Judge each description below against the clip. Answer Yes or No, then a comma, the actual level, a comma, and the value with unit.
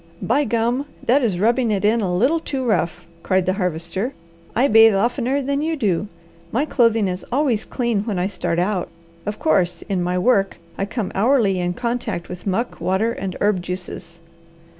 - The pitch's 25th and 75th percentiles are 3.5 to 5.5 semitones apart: Yes, average, 4.8 semitones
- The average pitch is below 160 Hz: No, high, 210 Hz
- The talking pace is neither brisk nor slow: Yes, average, 180 wpm